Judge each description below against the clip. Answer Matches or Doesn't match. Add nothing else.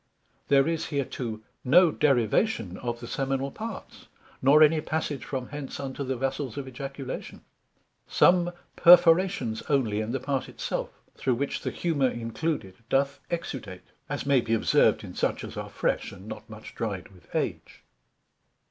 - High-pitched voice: Doesn't match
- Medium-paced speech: Matches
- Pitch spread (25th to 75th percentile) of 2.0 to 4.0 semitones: Doesn't match